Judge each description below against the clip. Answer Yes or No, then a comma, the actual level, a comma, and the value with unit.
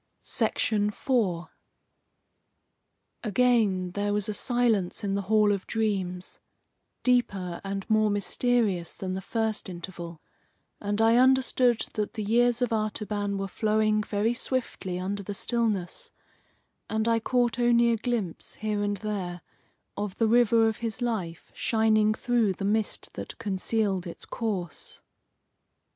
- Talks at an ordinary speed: No, slow, 130 wpm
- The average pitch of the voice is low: No, high, 215 Hz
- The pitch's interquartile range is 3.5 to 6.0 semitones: No, average, 2.8 semitones